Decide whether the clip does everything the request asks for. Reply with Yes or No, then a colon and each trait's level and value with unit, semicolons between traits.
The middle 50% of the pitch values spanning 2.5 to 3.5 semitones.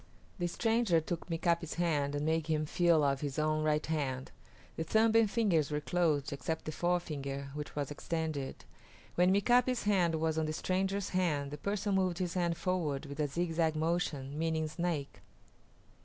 Yes: average, 3.1 semitones